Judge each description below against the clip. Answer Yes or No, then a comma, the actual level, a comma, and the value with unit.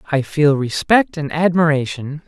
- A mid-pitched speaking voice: Yes, medium, 150 Hz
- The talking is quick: No, slow, 130 wpm